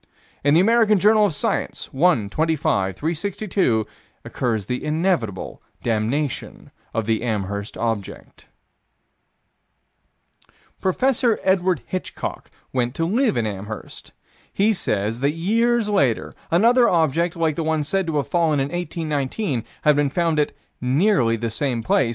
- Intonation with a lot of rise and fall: Yes, wide, 8.1 semitones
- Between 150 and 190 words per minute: No, slow, 135 wpm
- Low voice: No, medium, 155 Hz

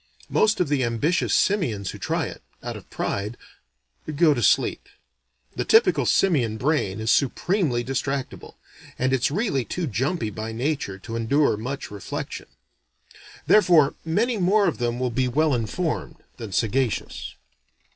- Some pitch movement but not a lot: No, wide, 6.2 semitones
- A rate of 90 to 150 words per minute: Yes, average, 145 wpm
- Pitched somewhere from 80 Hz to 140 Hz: Yes, low, 135 Hz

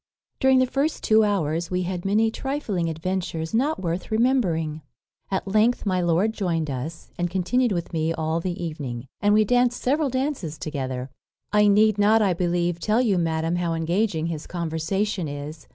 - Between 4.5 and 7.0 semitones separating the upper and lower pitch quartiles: Yes, average, 4.9 semitones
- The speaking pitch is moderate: Yes, medium, 180 Hz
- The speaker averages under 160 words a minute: No, average, 170 wpm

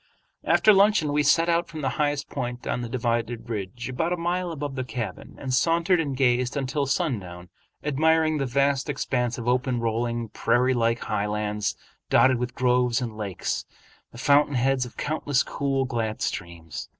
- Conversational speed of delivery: Yes, average, 170 wpm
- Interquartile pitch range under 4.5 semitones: Yes, average, 3.8 semitones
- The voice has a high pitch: No, low, 130 Hz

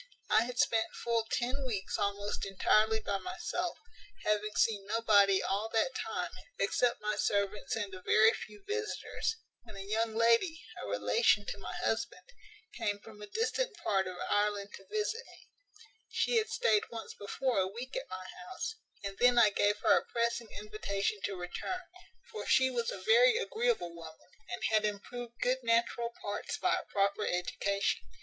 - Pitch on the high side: Yes, high, 215 Hz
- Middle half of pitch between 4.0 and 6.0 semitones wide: No, average, 3.6 semitones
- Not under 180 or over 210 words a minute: No, average, 170 wpm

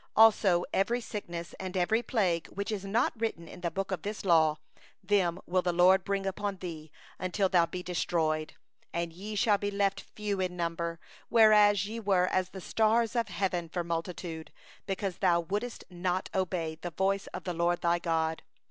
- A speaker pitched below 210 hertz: Yes, medium, 185 Hz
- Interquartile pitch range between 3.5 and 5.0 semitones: No, average, 3.0 semitones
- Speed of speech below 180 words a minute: No, average, 185 wpm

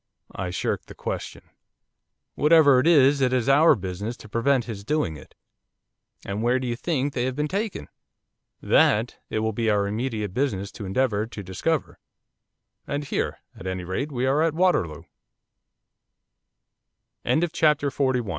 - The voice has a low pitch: Yes, low, 125 Hz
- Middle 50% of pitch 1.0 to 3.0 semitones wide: No, wide, 5.4 semitones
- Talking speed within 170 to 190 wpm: No, average, 145 wpm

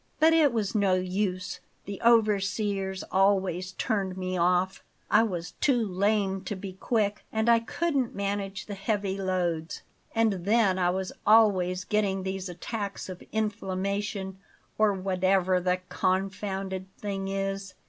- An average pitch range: No, narrow, 2.0 semitones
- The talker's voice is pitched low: No, high, 195 Hz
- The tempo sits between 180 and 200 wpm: No, average, 140 wpm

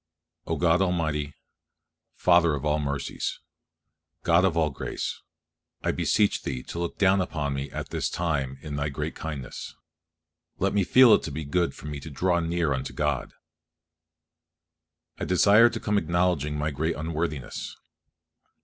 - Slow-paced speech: No, average, 155 wpm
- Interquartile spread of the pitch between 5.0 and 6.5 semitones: No, average, 3.5 semitones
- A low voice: Yes, very low, 80 Hz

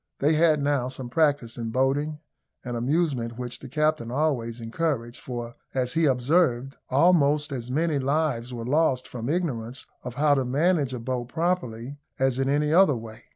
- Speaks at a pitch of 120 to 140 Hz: Yes, low, 135 Hz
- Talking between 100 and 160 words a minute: No, average, 170 wpm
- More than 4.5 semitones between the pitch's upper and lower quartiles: No, average, 3.9 semitones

